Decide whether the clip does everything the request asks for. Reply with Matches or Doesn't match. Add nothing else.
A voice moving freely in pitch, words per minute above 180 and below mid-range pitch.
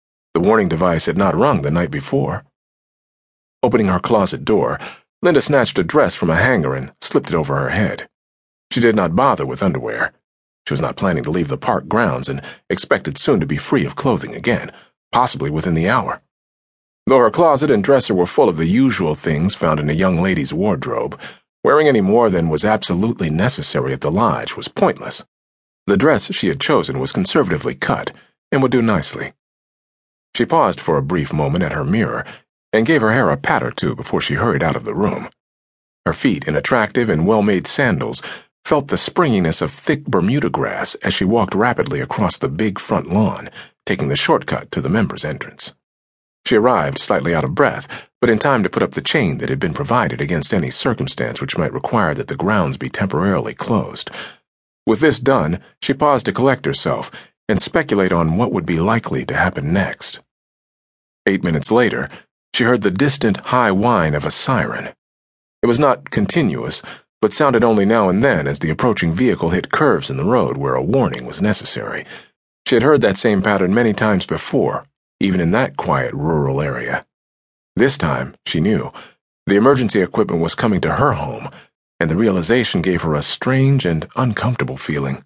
Matches